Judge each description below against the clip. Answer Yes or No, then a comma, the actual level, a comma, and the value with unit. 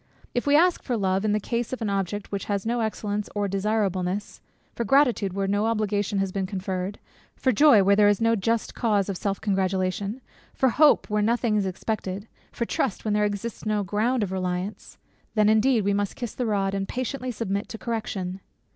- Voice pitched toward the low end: No, high, 205 Hz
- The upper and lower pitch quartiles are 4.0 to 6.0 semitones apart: No, average, 2.7 semitones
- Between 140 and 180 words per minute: No, average, 200 wpm